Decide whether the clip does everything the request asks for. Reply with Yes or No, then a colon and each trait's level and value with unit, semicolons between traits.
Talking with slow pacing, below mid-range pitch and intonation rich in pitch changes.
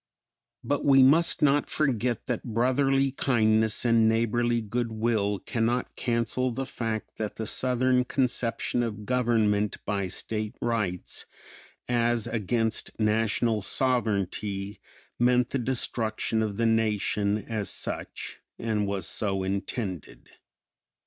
No: slow, 115 wpm; low, 115 Hz; narrow, 2.6 semitones